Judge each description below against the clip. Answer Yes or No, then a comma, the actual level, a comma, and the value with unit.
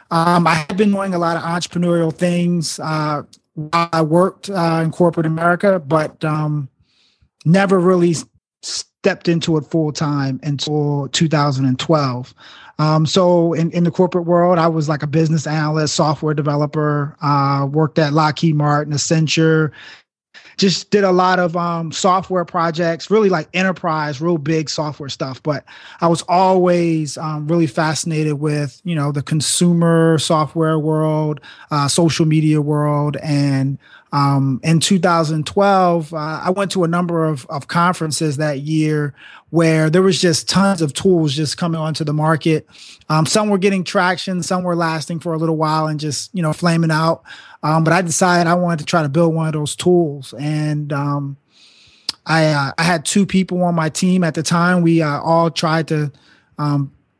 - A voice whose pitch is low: No, medium, 160 Hz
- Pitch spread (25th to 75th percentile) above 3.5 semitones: No, narrow, 2.4 semitones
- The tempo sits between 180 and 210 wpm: No, average, 170 wpm